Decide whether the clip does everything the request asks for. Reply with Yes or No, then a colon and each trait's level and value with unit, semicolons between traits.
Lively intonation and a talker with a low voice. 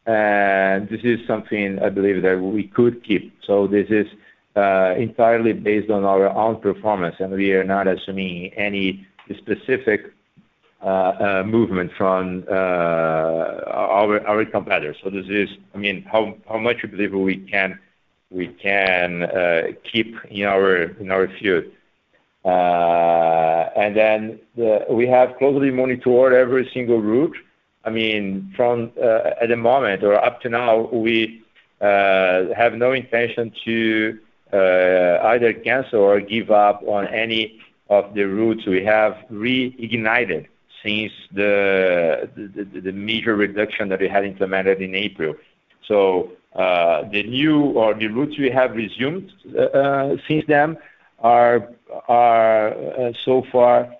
No: average, 3.2 semitones; low, 105 Hz